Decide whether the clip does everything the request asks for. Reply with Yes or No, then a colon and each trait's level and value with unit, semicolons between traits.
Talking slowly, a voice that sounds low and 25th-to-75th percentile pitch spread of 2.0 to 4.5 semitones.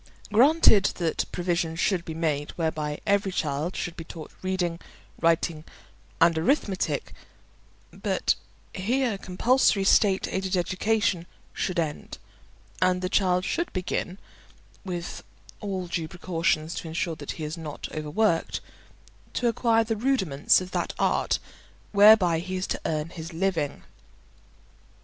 No: slow, 130 wpm; medium, 180 Hz; average, 3.3 semitones